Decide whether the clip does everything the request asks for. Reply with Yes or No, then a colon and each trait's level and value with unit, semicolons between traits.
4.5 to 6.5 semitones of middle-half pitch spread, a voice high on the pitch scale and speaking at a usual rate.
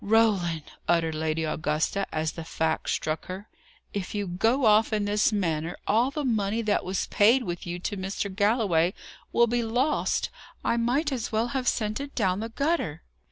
Yes: average, 5.0 semitones; high, 205 Hz; average, 180 wpm